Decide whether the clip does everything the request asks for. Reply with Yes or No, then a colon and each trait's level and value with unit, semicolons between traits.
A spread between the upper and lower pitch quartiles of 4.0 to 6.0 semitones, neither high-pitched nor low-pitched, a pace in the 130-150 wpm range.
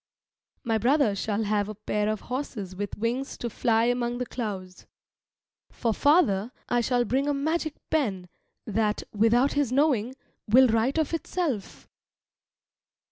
No: average, 4.4 semitones; high, 235 Hz; average, 140 wpm